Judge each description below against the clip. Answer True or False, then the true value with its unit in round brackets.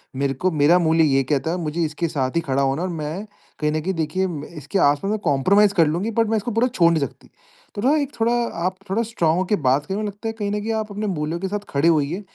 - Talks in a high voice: False (175 Hz)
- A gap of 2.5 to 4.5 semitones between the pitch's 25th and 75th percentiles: False (5.4 semitones)